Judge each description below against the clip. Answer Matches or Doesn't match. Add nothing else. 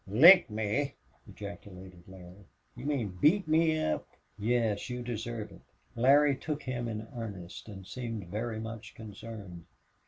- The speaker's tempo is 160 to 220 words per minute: Doesn't match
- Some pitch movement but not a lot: Matches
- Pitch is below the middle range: Matches